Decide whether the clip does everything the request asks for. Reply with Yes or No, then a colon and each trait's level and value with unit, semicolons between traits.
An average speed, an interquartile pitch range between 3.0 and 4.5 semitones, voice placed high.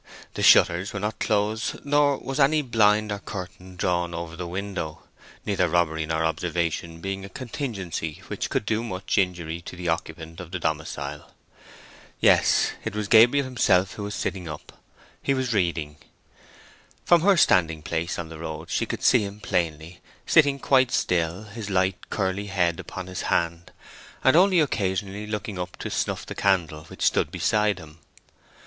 No: average, 165 wpm; average, 4.1 semitones; very low, 95 Hz